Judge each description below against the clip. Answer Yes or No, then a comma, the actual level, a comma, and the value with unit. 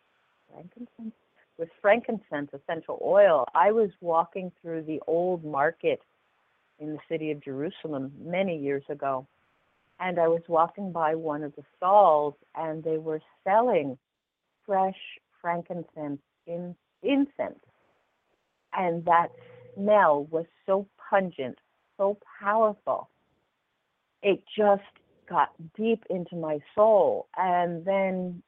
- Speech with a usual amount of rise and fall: Yes, average, 4.6 semitones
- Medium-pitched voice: Yes, medium, 170 Hz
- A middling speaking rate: No, slow, 115 wpm